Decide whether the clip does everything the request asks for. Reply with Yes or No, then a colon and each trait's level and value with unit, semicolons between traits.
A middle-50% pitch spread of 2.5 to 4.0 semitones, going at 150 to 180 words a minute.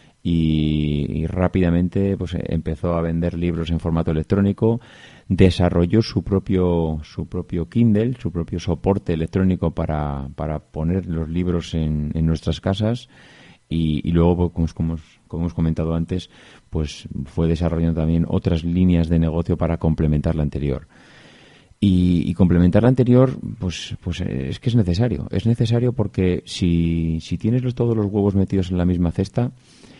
Yes: average, 3.2 semitones; average, 155 wpm